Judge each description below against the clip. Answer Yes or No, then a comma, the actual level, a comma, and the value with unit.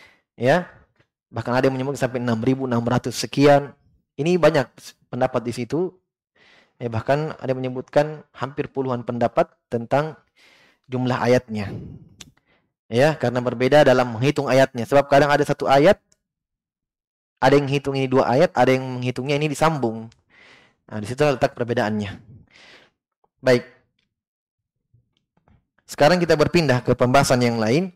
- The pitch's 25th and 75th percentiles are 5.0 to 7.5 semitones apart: No, average, 3.1 semitones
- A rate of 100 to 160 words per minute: Yes, average, 130 wpm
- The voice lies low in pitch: Yes, low, 130 Hz